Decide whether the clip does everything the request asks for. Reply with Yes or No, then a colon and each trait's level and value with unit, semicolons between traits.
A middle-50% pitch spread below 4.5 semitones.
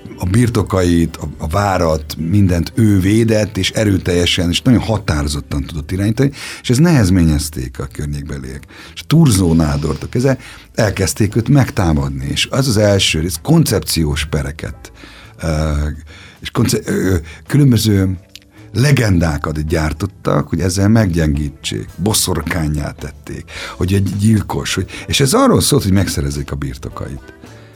No: wide, 5.5 semitones